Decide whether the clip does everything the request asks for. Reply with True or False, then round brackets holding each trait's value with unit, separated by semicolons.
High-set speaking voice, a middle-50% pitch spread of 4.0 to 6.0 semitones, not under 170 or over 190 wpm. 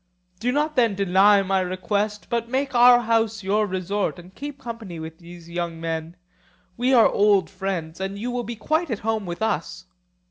True (205 Hz; 4.3 semitones; 185 wpm)